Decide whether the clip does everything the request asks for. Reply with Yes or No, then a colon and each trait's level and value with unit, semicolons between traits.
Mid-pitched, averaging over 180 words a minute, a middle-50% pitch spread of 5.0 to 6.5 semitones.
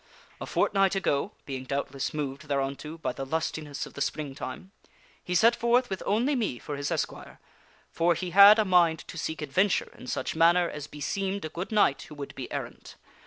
Yes: medium, 160 Hz; average, 190 wpm; wide, 5.5 semitones